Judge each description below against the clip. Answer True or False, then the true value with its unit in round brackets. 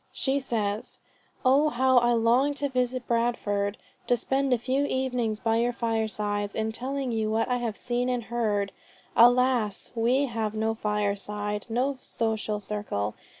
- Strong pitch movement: False (2.9 semitones)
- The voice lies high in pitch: True (230 Hz)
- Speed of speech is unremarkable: True (150 wpm)